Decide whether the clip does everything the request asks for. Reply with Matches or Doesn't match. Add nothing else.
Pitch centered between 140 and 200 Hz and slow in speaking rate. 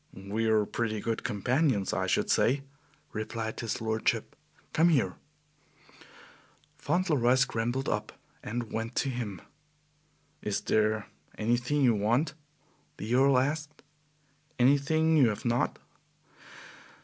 Doesn't match